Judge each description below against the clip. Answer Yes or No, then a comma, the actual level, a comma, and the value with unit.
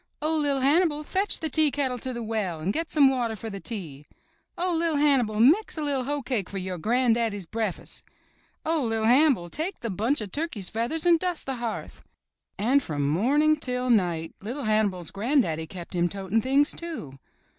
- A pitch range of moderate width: No, wide, 6.7 semitones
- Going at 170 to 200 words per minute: Yes, average, 190 wpm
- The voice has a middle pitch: No, high, 245 Hz